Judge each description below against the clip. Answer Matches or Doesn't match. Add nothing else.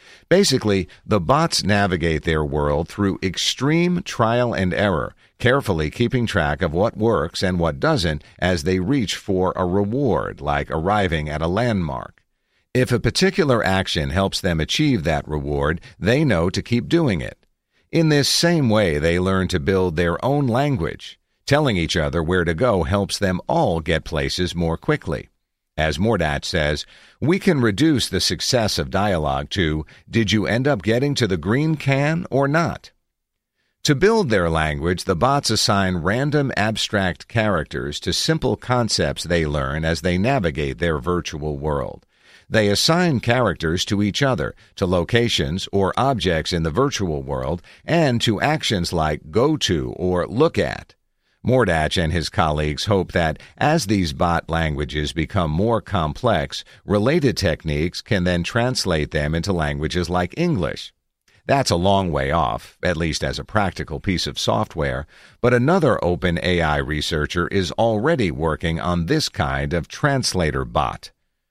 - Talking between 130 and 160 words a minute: Matches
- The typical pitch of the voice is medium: Doesn't match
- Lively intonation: Matches